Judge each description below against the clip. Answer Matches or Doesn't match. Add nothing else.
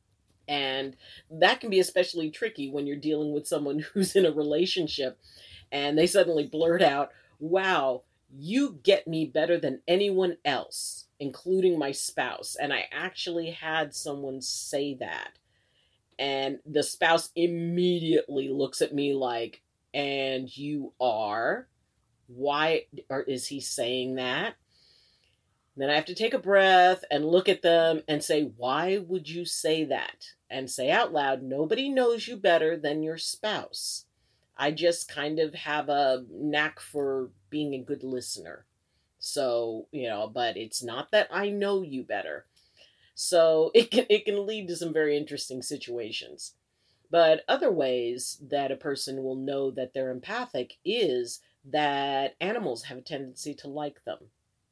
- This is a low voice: Doesn't match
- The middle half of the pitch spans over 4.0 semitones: Matches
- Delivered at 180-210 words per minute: Doesn't match